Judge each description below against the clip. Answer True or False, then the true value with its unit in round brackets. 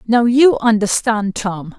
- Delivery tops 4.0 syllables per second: False (3.6 syllables/s)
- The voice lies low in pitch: False (220 Hz)